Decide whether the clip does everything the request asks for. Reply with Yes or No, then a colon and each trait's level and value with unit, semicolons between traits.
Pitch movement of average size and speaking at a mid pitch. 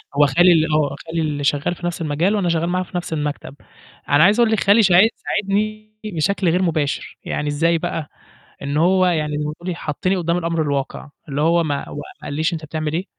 Yes: average, 3.4 semitones; medium, 165 Hz